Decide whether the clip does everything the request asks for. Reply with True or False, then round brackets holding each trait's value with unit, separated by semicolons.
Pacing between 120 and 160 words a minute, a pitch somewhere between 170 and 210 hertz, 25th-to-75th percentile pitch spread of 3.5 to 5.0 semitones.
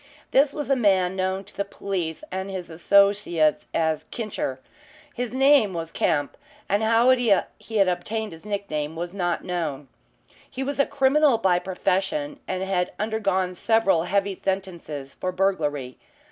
True (155 wpm; 190 Hz; 4.1 semitones)